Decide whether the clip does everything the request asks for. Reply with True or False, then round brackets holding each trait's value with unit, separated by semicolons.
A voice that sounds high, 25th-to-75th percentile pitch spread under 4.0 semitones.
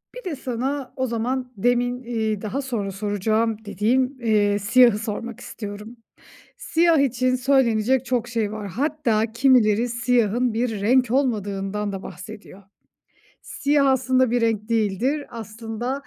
True (235 Hz; 3.2 semitones)